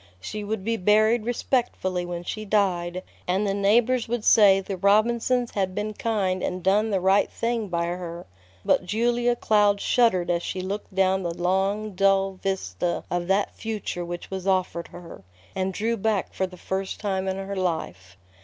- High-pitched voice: Yes, high, 195 Hz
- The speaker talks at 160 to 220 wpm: Yes, average, 175 wpm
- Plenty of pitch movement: No, average, 2.8 semitones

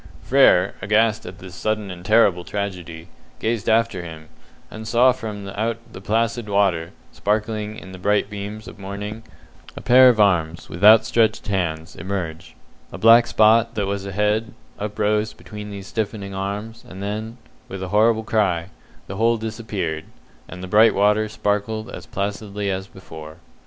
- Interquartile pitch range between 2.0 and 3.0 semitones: Yes, narrow, 2.5 semitones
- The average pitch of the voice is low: Yes, low, 105 Hz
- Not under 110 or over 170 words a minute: Yes, average, 160 wpm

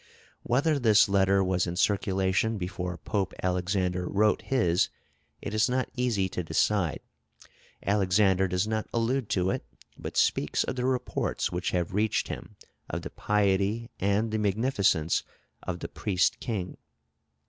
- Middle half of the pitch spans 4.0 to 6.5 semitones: No, average, 3.2 semitones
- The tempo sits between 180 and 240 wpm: No, average, 145 wpm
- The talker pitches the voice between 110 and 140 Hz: No, low, 100 Hz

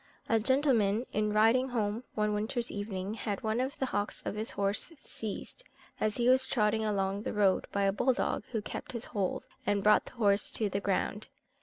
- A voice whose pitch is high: Yes, high, 215 Hz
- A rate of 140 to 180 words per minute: No, average, 200 wpm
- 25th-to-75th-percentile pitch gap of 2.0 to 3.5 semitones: Yes, narrow, 2.6 semitones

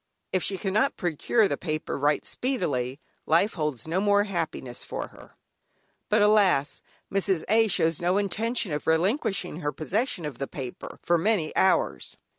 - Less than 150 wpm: No, average, 155 wpm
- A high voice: No, medium, 180 Hz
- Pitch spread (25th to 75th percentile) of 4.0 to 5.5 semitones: Yes, average, 5.2 semitones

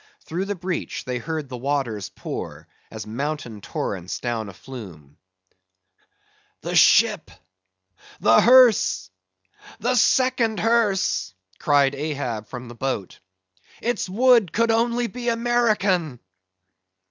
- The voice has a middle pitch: Yes, medium, 150 Hz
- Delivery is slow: Yes, slow, 110 wpm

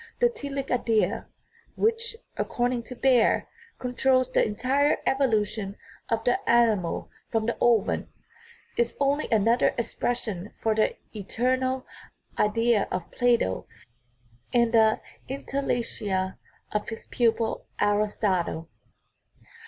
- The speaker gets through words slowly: Yes, slow, 115 wpm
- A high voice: Yes, high, 235 Hz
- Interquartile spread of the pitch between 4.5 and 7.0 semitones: No, average, 3.4 semitones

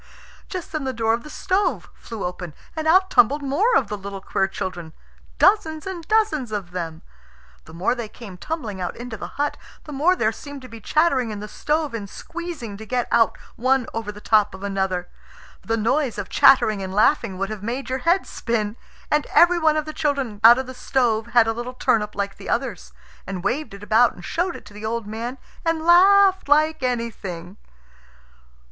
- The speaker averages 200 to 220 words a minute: Yes, fast, 205 wpm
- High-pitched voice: Yes, high, 235 Hz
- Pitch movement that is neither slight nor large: No, wide, 6.7 semitones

